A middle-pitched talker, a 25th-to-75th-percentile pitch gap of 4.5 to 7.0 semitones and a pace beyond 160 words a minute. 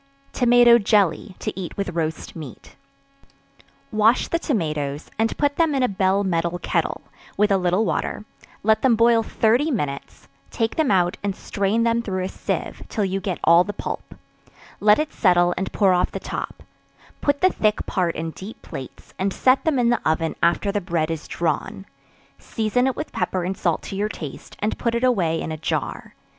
No: high, 200 Hz; average, 5.0 semitones; average, 190 wpm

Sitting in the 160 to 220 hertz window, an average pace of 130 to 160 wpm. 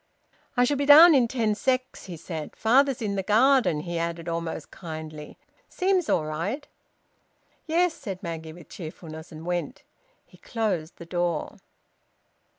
Yes: medium, 185 Hz; average, 150 wpm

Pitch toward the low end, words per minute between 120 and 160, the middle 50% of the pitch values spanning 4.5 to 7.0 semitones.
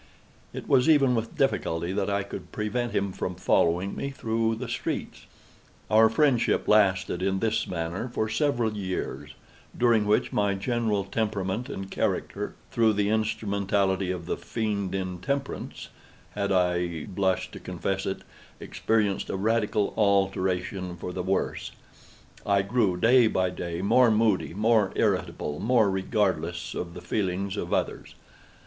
No: low, 100 Hz; average, 140 wpm; average, 3.2 semitones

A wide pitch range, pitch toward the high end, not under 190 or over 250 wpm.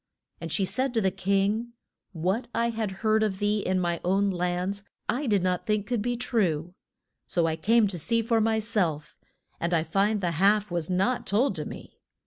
No: average, 3.8 semitones; high, 200 Hz; average, 200 wpm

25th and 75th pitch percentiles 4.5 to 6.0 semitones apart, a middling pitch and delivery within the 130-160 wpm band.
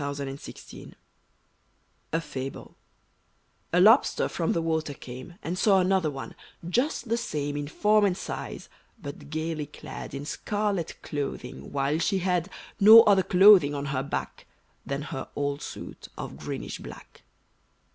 Yes: average, 5.1 semitones; medium, 160 Hz; average, 145 wpm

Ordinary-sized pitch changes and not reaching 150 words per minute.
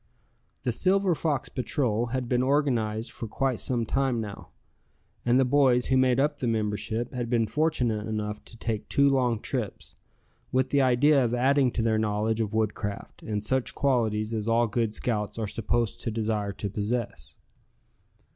No: average, 3.2 semitones; average, 170 wpm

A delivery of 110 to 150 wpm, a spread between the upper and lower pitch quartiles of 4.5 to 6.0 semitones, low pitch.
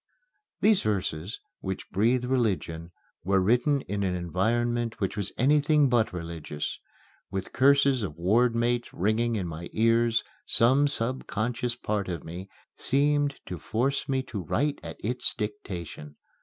Yes: average, 140 wpm; average, 5.2 semitones; low, 115 Hz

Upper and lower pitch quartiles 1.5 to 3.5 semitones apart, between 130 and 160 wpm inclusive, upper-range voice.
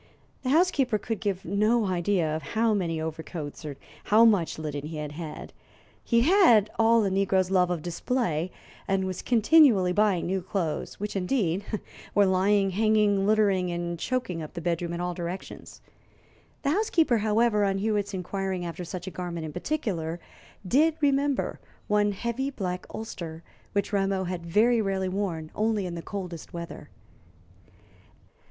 No: average, 4.0 semitones; average, 155 wpm; high, 195 Hz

